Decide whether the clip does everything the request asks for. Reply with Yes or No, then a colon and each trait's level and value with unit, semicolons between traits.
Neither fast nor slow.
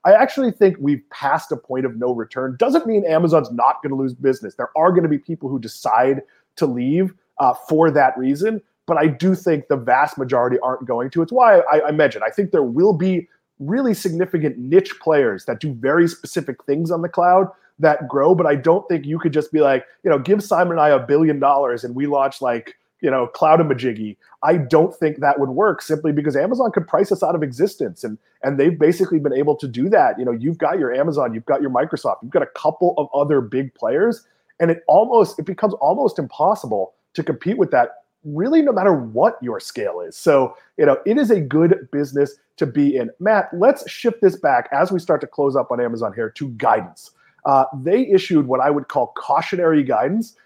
No: fast, 225 wpm